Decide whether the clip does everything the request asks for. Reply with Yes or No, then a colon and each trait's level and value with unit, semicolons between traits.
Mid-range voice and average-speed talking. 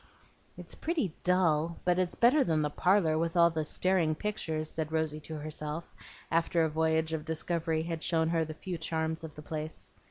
Yes: medium, 160 Hz; average, 190 wpm